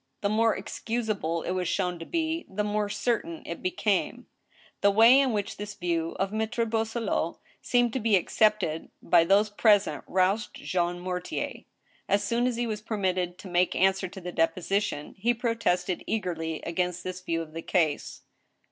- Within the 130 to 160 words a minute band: No, average, 175 wpm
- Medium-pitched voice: No, high, 195 Hz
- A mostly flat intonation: No, average, 3.8 semitones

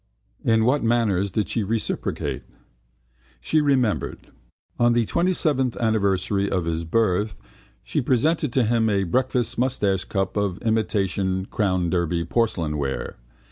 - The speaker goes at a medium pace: No, slow, 125 wpm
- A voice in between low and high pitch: No, low, 110 Hz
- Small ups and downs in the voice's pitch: No, average, 4.2 semitones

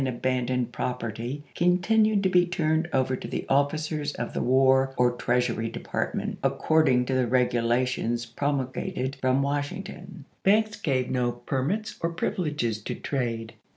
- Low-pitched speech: Yes, low, 130 Hz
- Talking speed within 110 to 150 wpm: Yes, slow, 135 wpm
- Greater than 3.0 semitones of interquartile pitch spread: Yes, average, 4.2 semitones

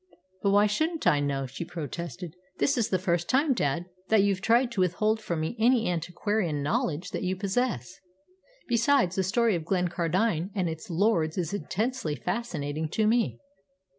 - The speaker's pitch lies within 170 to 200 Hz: Yes, medium, 185 Hz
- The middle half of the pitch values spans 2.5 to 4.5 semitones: No, average, 5.2 semitones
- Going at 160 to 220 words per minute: Yes, average, 165 wpm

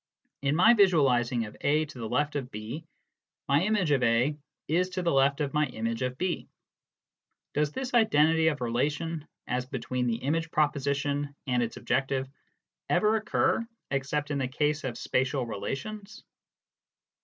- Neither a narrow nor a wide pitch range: Yes, average, 4.1 semitones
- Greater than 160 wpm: No, average, 155 wpm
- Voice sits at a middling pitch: Yes, medium, 145 Hz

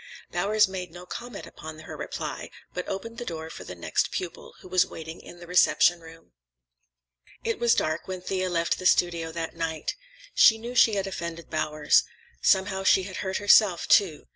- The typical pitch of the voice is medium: Yes, medium, 180 Hz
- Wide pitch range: No, average, 2.9 semitones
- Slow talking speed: No, average, 185 wpm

